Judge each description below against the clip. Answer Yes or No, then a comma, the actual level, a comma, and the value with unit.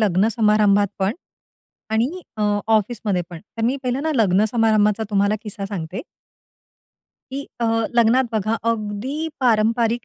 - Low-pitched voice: No, high, 215 Hz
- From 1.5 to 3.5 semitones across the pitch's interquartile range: Yes, narrow, 2.4 semitones